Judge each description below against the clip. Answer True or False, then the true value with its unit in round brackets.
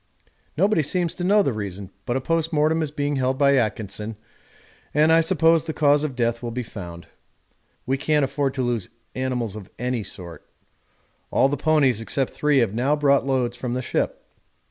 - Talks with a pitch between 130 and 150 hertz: True (135 Hz)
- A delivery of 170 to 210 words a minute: True (190 wpm)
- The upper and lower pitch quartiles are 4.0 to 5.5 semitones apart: True (4.3 semitones)